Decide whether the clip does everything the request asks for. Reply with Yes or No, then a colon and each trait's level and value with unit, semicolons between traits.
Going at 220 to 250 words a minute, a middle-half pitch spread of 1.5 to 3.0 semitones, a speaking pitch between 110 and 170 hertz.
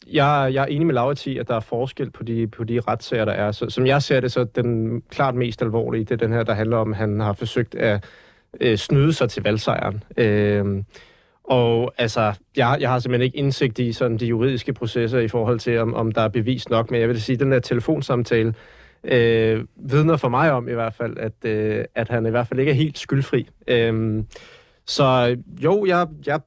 Yes: fast, 225 wpm; average, 2.7 semitones; low, 120 Hz